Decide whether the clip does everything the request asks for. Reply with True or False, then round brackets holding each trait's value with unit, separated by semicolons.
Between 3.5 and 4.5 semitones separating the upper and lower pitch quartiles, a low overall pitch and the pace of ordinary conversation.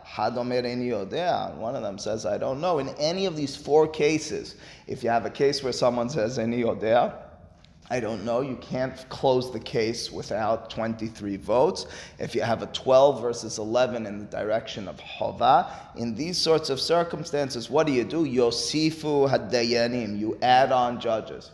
True (4.0 semitones; 125 Hz; 160 wpm)